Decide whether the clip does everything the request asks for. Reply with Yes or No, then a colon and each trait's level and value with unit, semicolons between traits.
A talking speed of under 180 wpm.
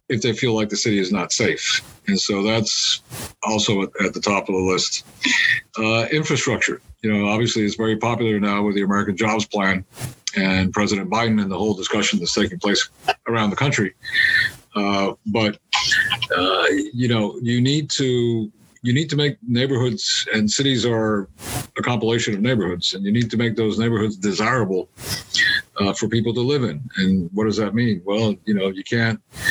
No: average, 185 wpm